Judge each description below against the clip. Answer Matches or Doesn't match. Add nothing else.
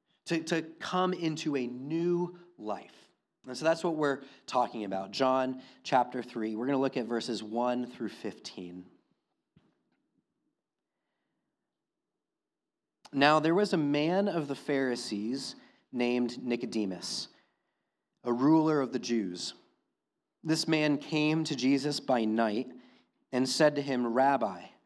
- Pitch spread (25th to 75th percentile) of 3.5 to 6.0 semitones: Matches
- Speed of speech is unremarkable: Doesn't match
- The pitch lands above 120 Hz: Matches